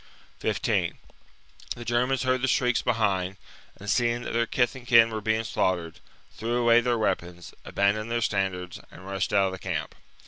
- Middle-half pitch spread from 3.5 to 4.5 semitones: Yes, average, 3.9 semitones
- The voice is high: No, low, 110 Hz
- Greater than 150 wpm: Yes, average, 185 wpm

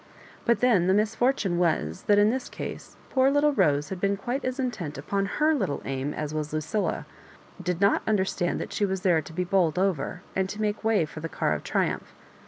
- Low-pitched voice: No, high, 190 Hz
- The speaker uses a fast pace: Yes, fast, 220 wpm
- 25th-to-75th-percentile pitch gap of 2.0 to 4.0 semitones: No, average, 5.0 semitones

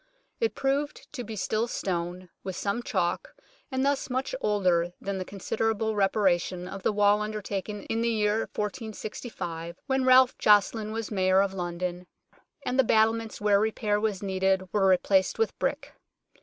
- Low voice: No, high, 210 Hz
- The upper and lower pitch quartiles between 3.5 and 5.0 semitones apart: No, average, 3.1 semitones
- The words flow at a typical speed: Yes, average, 155 wpm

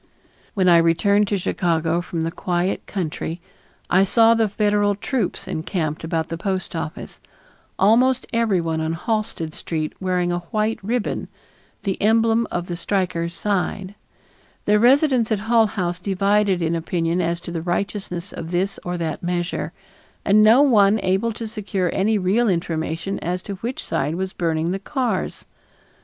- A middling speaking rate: Yes, average, 155 wpm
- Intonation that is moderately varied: Yes, average, 3.8 semitones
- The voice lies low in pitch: No, medium, 185 Hz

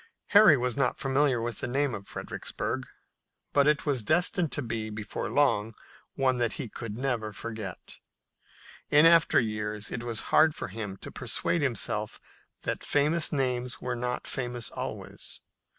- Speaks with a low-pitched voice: Yes, low, 125 Hz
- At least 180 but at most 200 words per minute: No, average, 155 wpm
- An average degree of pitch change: Yes, average, 4.6 semitones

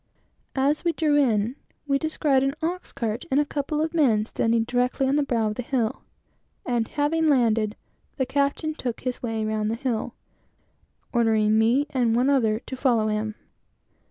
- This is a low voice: No, very high, 250 Hz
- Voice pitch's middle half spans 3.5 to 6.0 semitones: Yes, average, 4.1 semitones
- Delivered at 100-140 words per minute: No, average, 175 wpm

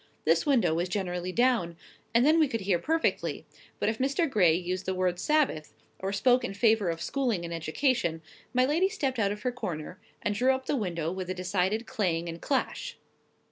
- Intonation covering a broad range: Yes, wide, 6.5 semitones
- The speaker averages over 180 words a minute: Yes, average, 200 wpm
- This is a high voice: Yes, high, 200 Hz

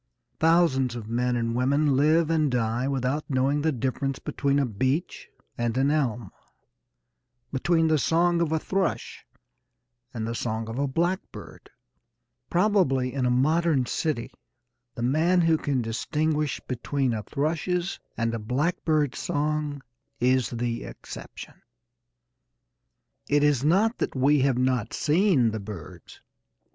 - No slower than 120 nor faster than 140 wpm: Yes, slow, 135 wpm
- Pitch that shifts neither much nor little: Yes, average, 4.2 semitones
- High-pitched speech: No, medium, 140 Hz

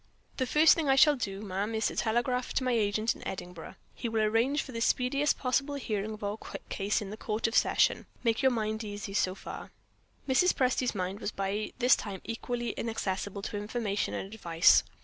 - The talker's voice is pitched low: No, high, 220 Hz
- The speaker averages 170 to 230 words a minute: Yes, average, 200 wpm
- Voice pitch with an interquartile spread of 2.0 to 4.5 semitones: Yes, average, 3.7 semitones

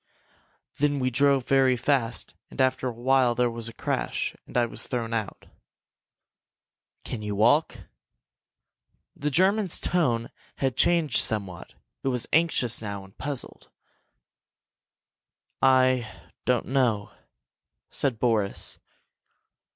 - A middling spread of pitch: Yes, average, 3.1 semitones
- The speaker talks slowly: Yes, slow, 115 wpm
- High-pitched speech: No, low, 125 Hz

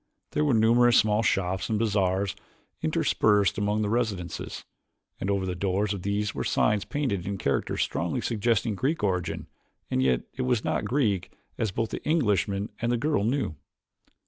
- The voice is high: No, low, 105 Hz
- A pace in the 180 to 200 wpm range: No, average, 170 wpm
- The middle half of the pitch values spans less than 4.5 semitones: Yes, average, 3.3 semitones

